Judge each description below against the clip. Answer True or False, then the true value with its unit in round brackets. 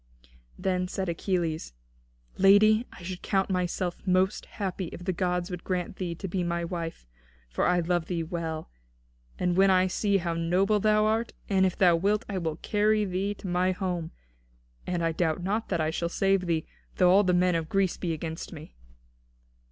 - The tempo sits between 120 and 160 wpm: False (190 wpm)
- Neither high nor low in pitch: True (180 Hz)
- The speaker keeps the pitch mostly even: True (2.3 semitones)